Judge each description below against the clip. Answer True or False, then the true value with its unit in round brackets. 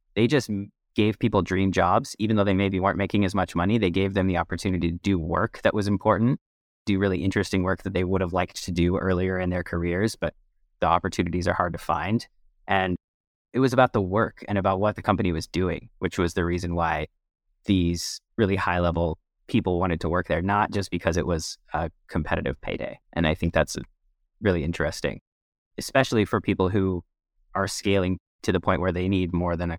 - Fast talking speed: True (210 wpm)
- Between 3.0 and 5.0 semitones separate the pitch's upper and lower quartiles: False (2.6 semitones)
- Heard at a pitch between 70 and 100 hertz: True (95 Hz)